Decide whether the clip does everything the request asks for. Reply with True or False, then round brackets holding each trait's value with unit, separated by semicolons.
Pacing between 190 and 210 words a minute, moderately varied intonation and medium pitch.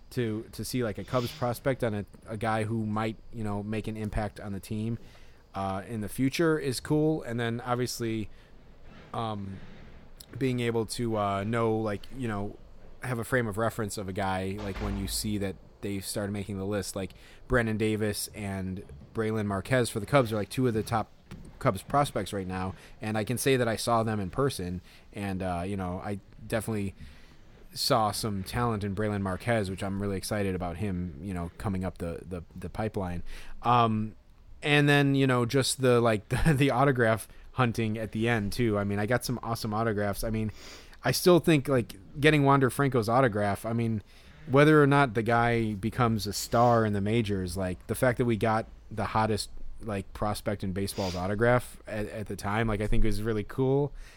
False (200 wpm; 3.2 semitones; 110 Hz)